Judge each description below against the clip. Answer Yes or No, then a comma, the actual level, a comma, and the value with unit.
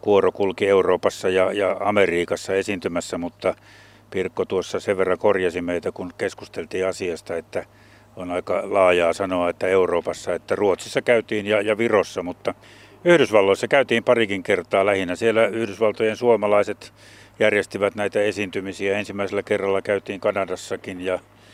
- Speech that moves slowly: No, average, 125 wpm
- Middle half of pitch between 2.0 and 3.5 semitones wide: Yes, narrow, 2.5 semitones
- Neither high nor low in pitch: No, low, 100 Hz